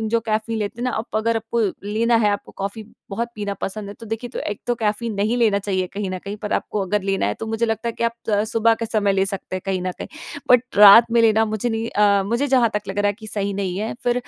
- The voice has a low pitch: No, high, 215 Hz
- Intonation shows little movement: Yes, narrow, 2.3 semitones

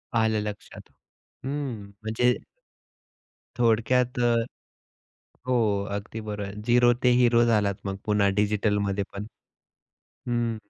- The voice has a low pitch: Yes, low, 110 Hz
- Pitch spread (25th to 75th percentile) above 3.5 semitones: No, average, 2.8 semitones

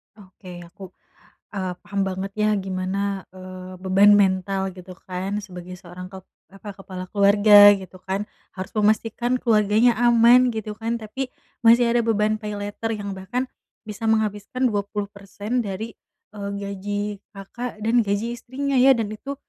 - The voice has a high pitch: Yes, high, 205 Hz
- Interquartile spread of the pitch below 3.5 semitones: Yes, average, 2.9 semitones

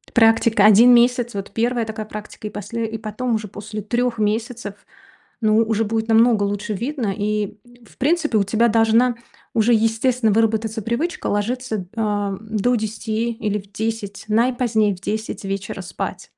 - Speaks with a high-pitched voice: Yes, high, 220 Hz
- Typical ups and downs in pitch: No, narrow, 2.1 semitones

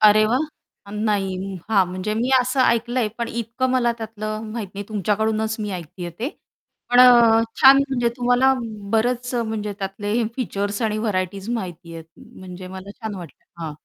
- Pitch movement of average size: Yes, average, 3.4 semitones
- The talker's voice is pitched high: Yes, high, 215 Hz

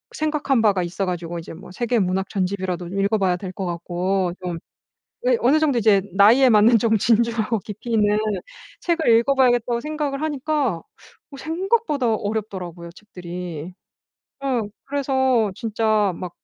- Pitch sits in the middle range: No, high, 215 Hz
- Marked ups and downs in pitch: Yes, wide, 6.0 semitones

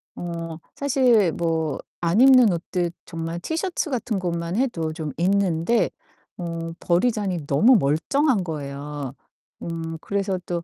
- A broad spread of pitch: No, average, 4.9 semitones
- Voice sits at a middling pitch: Yes, medium, 175 Hz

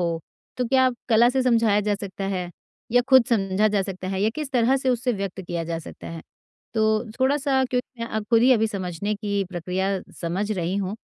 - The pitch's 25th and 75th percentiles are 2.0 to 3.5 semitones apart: No, average, 4.4 semitones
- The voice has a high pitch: Yes, high, 210 Hz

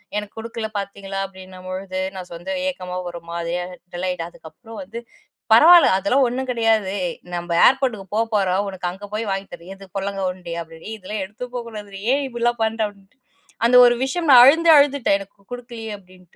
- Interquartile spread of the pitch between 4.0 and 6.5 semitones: Yes, average, 4.3 semitones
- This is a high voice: Yes, high, 200 Hz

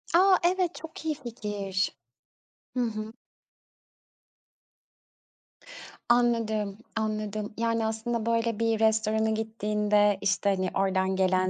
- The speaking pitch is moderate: No, high, 220 Hz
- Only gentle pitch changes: Yes, narrow, 2.0 semitones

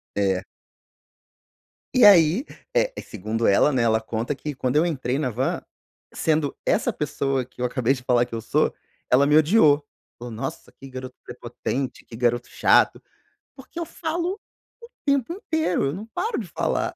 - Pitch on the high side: No, low, 135 Hz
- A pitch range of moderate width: No, wide, 8.0 semitones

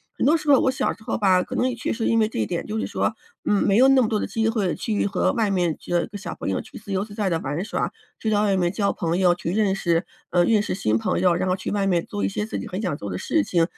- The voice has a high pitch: Yes, high, 195 Hz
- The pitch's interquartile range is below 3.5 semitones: No, average, 4.0 semitones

